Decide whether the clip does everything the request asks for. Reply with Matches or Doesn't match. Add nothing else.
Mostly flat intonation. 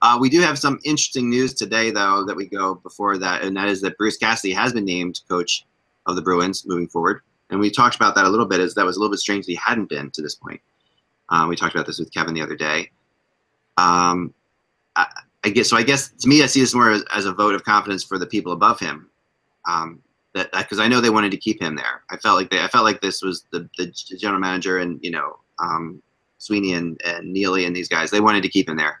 Doesn't match